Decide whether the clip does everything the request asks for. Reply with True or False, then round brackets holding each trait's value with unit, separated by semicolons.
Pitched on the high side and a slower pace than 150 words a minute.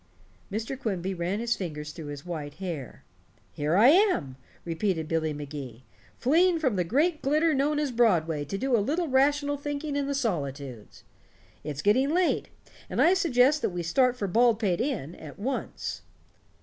False (215 Hz; 165 wpm)